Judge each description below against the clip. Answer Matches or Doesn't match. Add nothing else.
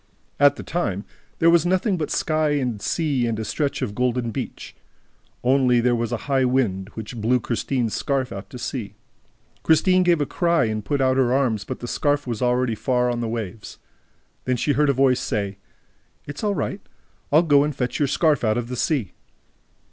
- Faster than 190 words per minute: Matches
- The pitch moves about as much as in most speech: Matches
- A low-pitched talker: Matches